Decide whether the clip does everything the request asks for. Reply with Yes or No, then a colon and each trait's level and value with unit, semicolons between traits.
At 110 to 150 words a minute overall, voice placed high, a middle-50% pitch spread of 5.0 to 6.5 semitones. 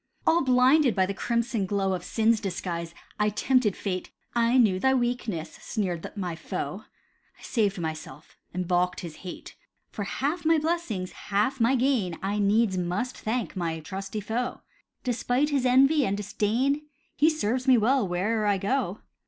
No: average, 160 wpm; high, 215 Hz; average, 5.3 semitones